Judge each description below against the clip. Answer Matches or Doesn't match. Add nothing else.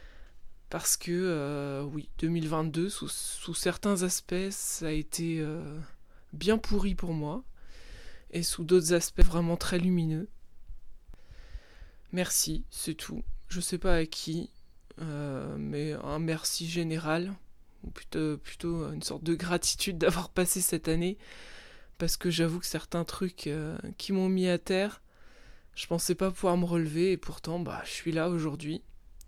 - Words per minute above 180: Doesn't match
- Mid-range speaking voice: Matches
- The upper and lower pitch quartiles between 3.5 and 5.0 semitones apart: Doesn't match